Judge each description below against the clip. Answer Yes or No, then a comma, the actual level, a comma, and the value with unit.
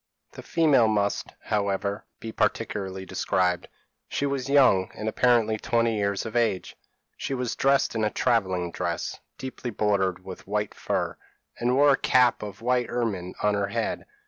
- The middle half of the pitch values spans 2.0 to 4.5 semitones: Yes, average, 4.0 semitones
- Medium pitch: No, low, 110 Hz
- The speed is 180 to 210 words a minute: No, average, 165 wpm